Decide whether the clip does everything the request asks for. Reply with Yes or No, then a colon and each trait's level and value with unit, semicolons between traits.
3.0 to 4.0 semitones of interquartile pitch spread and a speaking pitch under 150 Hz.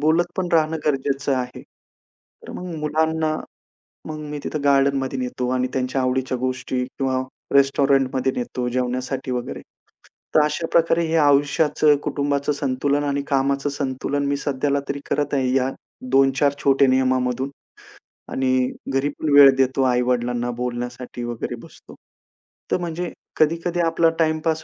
No: narrow, 2.6 semitones; medium, 140 Hz